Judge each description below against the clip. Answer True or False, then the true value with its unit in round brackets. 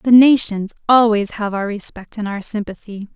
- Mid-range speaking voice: False (210 Hz)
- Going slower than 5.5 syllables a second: True (4.8 syllables/s)